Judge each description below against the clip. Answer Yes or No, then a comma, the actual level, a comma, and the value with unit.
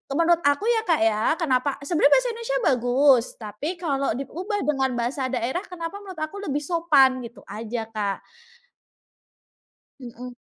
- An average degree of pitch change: No, wide, 5.7 semitones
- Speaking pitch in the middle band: No, very high, 280 Hz